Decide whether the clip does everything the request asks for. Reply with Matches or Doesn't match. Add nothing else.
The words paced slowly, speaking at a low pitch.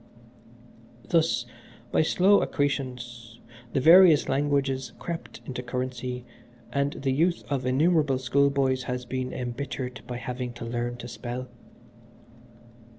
Matches